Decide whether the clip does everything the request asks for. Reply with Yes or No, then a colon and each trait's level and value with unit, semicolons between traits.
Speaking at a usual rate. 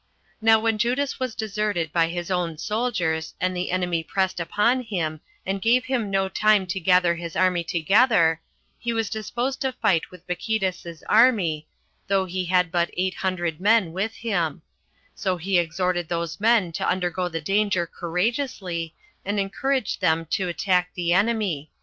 Yes: average, 160 wpm